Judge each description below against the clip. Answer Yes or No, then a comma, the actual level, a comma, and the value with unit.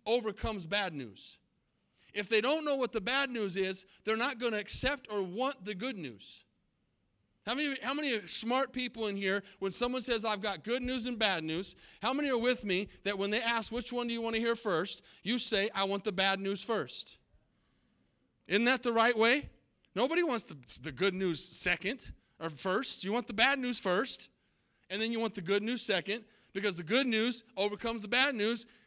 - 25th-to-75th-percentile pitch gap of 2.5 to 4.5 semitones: Yes, average, 3.6 semitones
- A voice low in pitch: No, high, 220 Hz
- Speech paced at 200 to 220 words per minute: Yes, fast, 205 wpm